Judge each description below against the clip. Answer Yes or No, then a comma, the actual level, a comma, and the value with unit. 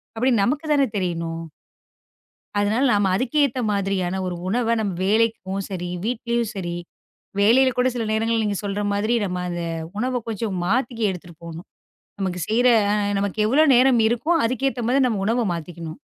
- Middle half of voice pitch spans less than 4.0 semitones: No, average, 4.6 semitones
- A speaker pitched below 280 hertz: Yes, high, 220 Hz